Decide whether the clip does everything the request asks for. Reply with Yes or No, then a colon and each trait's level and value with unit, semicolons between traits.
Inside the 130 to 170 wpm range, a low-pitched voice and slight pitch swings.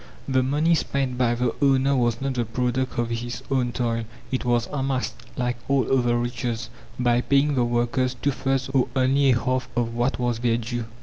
No: average, 195 wpm; low, 125 Hz; narrow, 1.9 semitones